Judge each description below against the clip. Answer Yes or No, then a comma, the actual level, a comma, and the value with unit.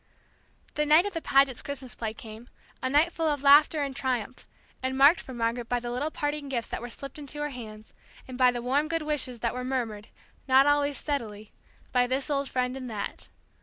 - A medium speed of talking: No, fast, 210 wpm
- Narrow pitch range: No, average, 3.2 semitones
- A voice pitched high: Yes, very high, 260 Hz